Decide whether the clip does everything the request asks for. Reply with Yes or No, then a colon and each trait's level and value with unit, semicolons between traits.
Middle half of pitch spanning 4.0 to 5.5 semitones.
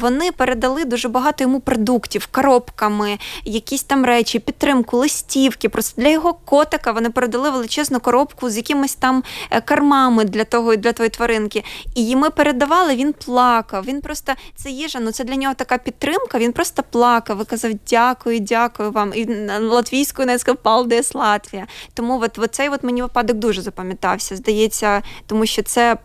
No: average, 3.2 semitones